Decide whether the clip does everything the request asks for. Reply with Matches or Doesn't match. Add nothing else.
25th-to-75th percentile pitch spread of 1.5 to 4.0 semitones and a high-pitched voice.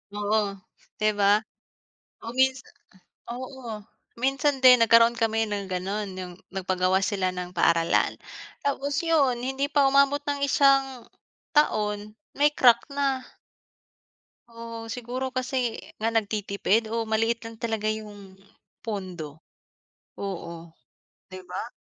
Doesn't match